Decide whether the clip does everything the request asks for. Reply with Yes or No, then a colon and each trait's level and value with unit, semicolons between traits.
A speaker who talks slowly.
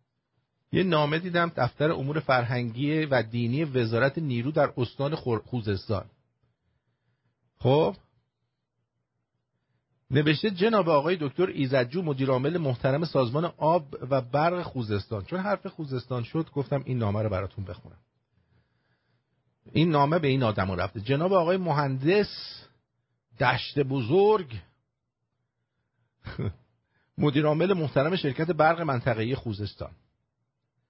Yes: slow, 105 wpm